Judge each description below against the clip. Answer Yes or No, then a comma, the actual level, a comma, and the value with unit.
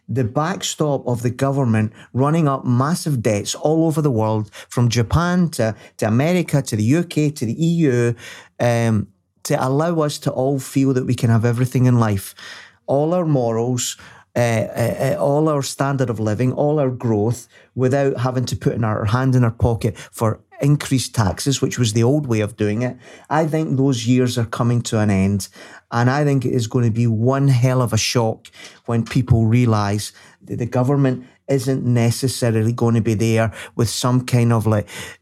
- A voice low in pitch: Yes, low, 125 Hz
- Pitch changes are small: No, average, 3.2 semitones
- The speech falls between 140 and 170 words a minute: No, average, 190 wpm